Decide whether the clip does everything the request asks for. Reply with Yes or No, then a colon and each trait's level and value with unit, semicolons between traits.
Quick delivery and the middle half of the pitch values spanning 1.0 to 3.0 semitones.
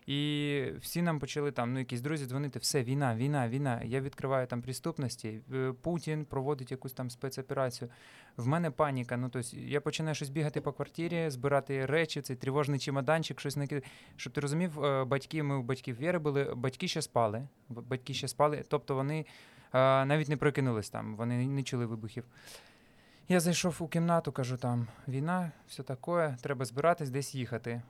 Yes: fast, 170 wpm; narrow, 2.5 semitones